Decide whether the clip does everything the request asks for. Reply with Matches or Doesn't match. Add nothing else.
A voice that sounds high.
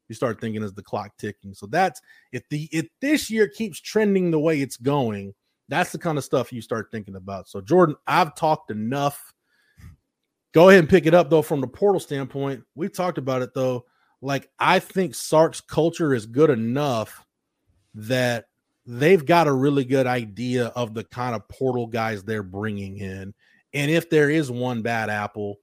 Doesn't match